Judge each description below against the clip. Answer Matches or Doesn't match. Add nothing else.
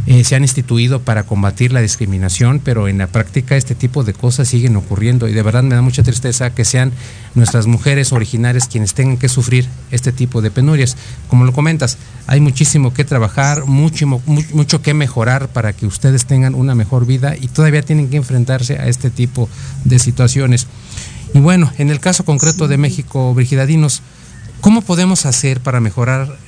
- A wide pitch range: Doesn't match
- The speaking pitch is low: Matches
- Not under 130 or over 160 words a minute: Doesn't match